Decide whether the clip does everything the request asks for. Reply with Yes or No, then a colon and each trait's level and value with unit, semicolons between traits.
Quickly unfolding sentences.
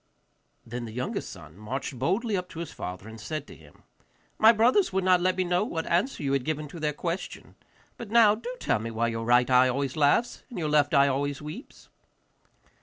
Yes: fast, 215 wpm